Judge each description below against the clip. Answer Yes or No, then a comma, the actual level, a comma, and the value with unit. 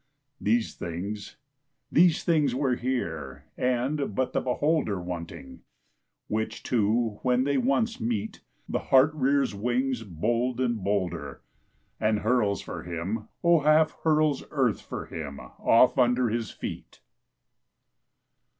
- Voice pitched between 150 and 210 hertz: No, low, 120 Hz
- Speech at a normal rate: No, slow, 125 wpm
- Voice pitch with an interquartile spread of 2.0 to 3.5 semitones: No, average, 4.9 semitones